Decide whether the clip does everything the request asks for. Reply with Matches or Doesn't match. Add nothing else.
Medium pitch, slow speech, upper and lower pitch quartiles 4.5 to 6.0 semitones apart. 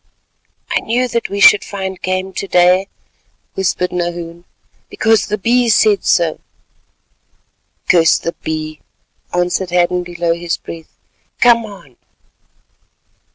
Doesn't match